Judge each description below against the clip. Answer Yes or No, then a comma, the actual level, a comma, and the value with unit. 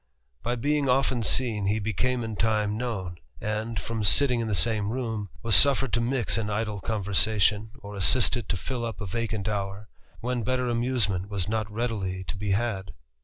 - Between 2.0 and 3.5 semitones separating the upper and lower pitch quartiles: Yes, average, 2.7 semitones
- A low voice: Yes, low, 110 Hz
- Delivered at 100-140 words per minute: No, average, 180 wpm